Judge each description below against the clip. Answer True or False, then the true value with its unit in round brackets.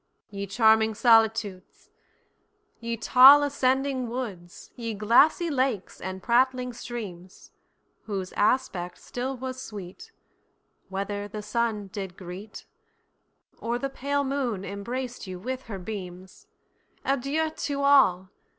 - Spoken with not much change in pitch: False (4.8 semitones)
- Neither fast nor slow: False (95 wpm)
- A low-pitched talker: False (230 Hz)